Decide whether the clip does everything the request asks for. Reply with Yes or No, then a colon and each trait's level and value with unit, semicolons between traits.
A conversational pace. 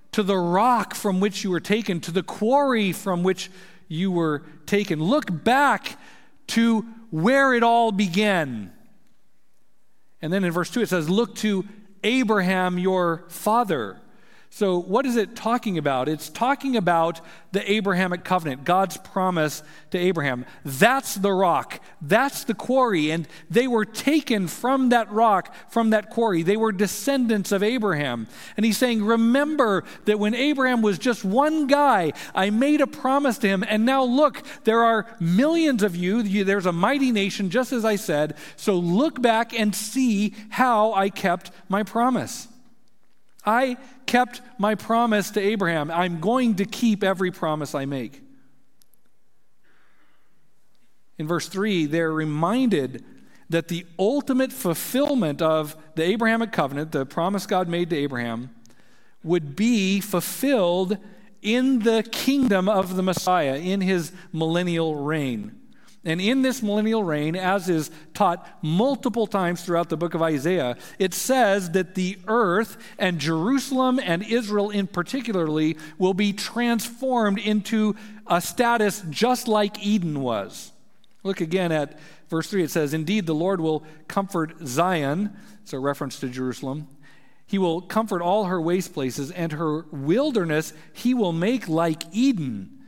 Yes: average, 150 wpm